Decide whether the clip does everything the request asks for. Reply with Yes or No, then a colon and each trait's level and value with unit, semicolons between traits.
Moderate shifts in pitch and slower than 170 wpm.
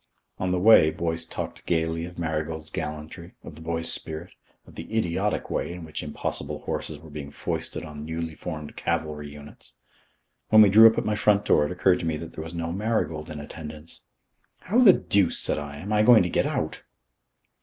No: average, 3.0 semitones; average, 200 wpm